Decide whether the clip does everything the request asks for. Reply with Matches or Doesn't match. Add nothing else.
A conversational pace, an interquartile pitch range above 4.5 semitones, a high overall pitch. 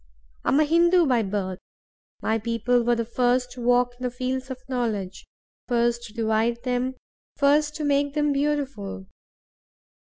Doesn't match